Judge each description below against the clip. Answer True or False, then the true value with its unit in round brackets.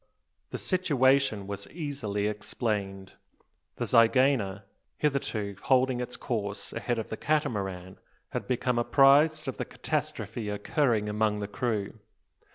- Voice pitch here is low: True (115 Hz)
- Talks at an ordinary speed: False (120 wpm)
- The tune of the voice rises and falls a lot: False (4.8 semitones)